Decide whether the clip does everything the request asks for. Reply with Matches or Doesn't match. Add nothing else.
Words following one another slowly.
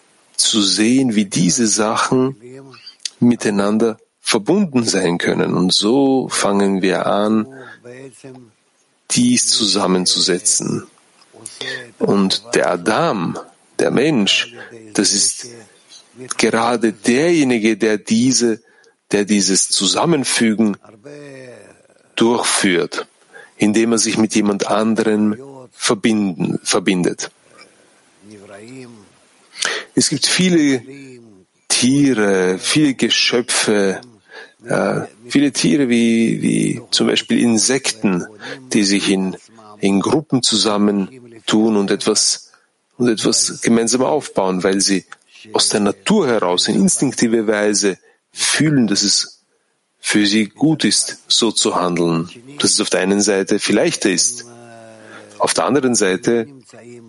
Matches